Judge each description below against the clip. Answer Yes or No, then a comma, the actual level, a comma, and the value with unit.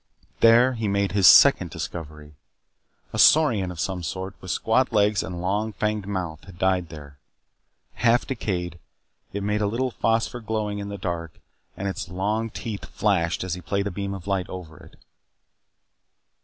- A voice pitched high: No, low, 100 Hz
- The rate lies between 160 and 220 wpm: Yes, average, 170 wpm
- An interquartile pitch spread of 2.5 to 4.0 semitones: Yes, average, 3.3 semitones